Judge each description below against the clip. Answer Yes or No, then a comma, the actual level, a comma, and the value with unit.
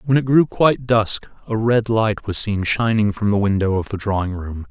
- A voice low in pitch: Yes, low, 110 Hz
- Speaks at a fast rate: Yes, fast, 230 wpm